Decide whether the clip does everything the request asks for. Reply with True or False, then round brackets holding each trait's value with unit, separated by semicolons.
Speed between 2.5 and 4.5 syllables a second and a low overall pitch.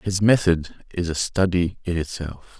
True (4.3 syllables/s; 90 Hz)